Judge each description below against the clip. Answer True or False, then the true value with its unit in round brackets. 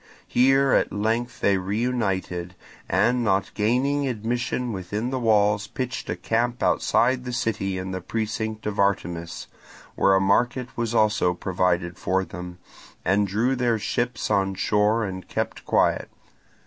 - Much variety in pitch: False (4.2 semitones)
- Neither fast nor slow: True (145 wpm)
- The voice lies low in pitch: True (105 Hz)